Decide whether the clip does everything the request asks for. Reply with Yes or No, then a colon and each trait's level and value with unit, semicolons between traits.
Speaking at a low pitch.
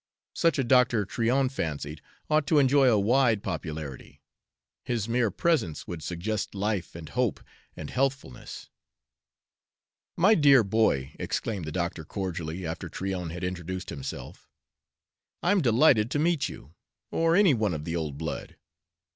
Yes: low, 105 Hz